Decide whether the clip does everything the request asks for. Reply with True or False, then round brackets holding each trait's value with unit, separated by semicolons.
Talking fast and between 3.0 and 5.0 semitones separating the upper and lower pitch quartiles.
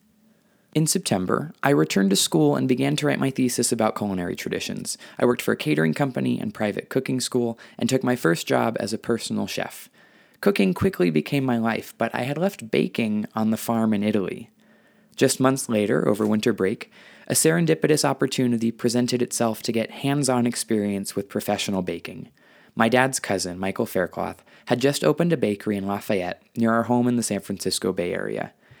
False (185 wpm; 4.5 semitones)